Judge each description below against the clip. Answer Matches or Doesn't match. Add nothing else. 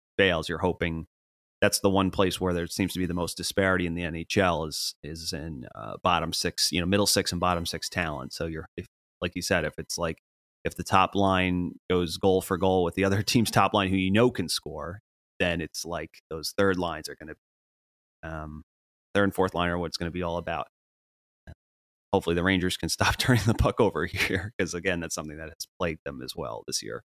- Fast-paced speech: Matches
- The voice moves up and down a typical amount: Matches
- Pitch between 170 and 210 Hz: Doesn't match